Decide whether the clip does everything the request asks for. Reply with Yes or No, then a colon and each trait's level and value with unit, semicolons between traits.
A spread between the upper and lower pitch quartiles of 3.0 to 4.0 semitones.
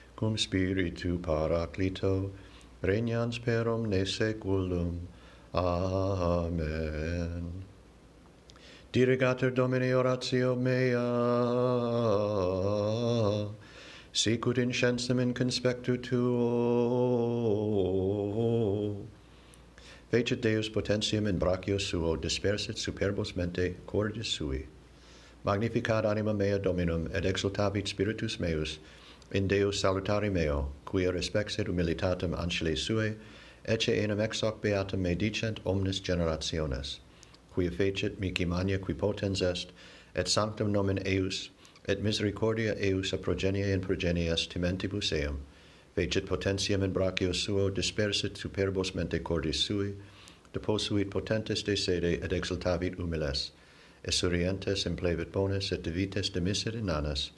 Yes: average, 3.5 semitones